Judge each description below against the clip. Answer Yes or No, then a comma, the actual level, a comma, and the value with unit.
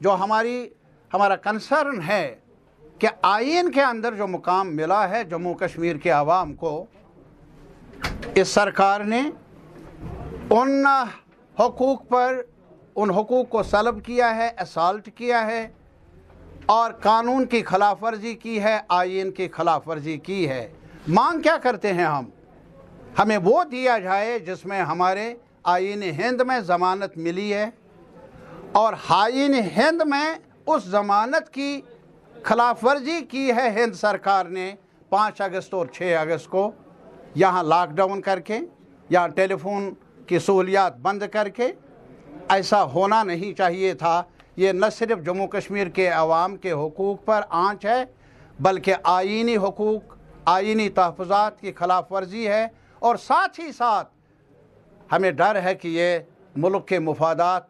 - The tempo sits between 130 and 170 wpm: Yes, average, 140 wpm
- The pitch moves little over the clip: No, average, 4.2 semitones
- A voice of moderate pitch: No, high, 200 Hz